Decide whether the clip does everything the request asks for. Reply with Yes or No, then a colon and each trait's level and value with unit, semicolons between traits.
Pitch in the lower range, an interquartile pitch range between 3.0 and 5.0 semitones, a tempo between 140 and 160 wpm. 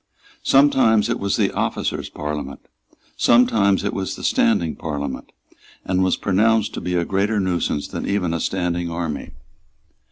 Yes: very low, 95 Hz; average, 3.7 semitones; average, 150 wpm